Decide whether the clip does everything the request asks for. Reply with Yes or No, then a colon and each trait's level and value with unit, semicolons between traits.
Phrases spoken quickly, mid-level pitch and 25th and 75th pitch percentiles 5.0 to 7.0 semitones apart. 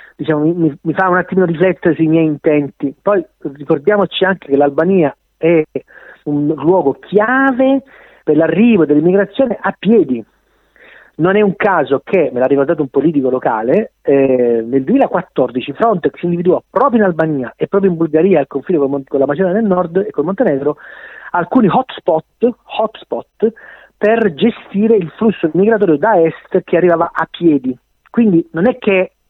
No: average, 160 wpm; medium, 175 Hz; average, 5.3 semitones